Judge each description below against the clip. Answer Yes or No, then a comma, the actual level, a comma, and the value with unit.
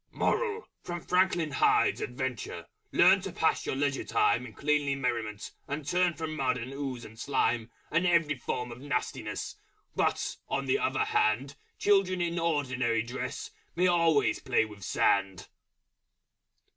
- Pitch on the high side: No, medium, 140 Hz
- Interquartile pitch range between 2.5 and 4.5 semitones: No, wide, 5.4 semitones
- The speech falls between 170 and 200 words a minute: No, average, 145 wpm